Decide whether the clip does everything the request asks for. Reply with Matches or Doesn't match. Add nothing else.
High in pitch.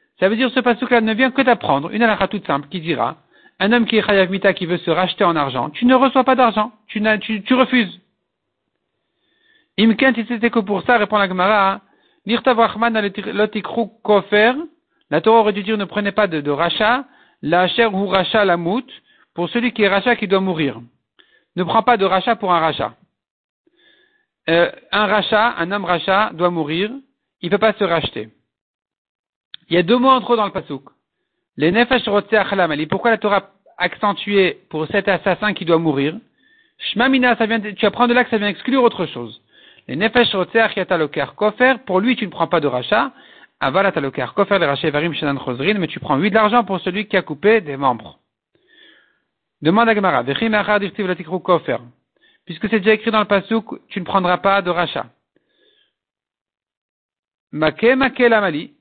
Matches